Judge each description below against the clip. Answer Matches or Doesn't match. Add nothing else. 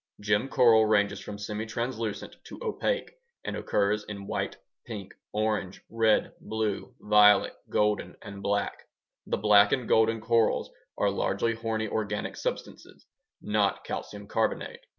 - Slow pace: Matches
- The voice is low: Matches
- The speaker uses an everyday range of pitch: Doesn't match